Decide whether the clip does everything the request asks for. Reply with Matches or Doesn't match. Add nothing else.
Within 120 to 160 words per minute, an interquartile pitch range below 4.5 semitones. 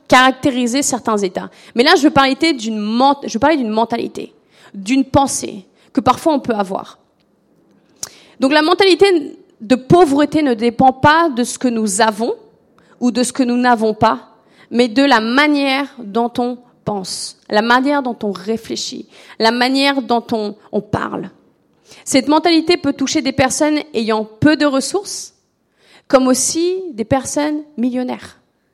Matches